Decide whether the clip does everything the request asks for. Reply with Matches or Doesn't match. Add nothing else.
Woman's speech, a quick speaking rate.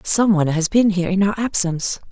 Matches